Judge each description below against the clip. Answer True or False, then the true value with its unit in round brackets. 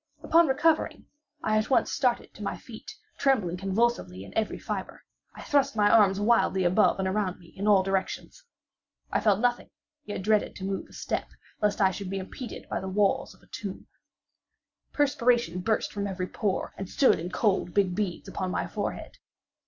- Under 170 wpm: False (185 wpm)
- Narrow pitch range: False (3.8 semitones)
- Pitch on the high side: True (205 Hz)